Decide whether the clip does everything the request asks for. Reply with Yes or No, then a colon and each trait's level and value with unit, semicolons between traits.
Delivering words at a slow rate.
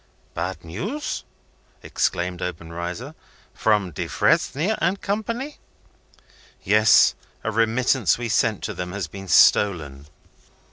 Yes: slow, 100 wpm